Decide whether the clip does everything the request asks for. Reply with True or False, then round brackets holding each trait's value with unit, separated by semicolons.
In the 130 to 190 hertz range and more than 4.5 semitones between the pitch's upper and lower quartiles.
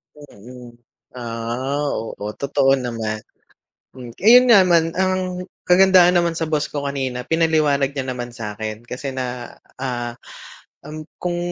True (140 Hz; 5.2 semitones)